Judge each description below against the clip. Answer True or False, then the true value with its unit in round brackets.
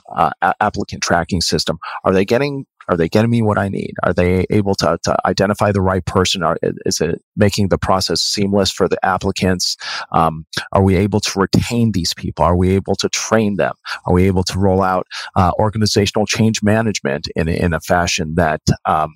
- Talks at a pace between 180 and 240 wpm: True (200 wpm)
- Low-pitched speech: True (95 Hz)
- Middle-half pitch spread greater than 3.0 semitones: False (2.6 semitones)